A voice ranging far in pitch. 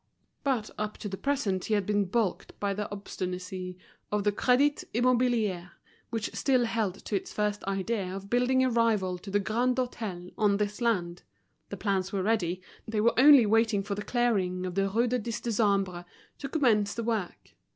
No: average, 3.4 semitones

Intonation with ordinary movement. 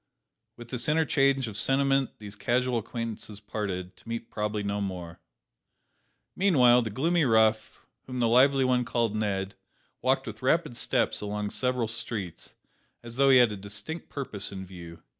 Yes: average, 3.8 semitones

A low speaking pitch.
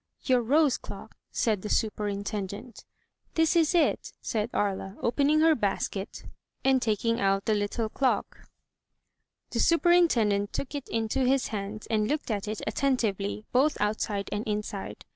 No: high, 220 Hz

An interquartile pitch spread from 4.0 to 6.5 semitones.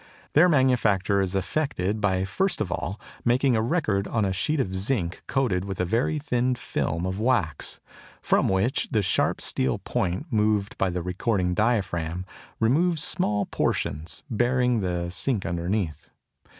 Yes: average, 5.3 semitones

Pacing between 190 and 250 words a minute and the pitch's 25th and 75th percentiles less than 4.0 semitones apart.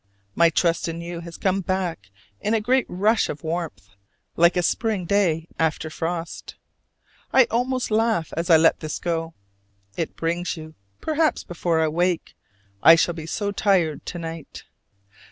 No: average, 160 wpm; average, 3.4 semitones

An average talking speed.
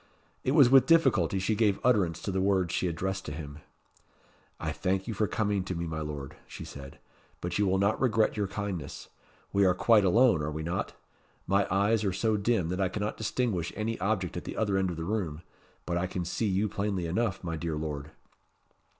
No: fast, 210 wpm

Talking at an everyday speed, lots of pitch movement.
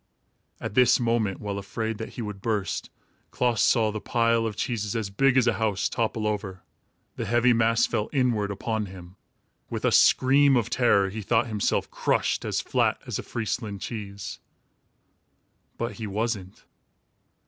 No: average, 160 wpm; narrow, 2.6 semitones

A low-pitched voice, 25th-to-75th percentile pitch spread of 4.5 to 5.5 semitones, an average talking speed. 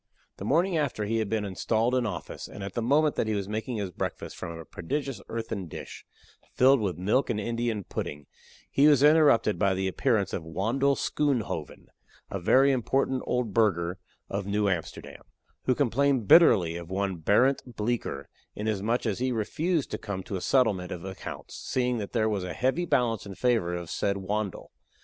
Yes: low, 110 Hz; average, 4.9 semitones; average, 185 wpm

